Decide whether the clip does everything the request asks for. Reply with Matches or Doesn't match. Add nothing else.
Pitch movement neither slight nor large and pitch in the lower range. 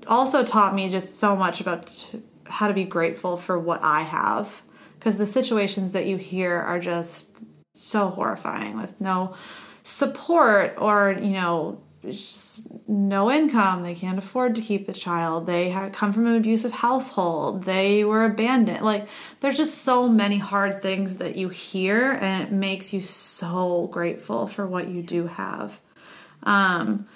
Doesn't match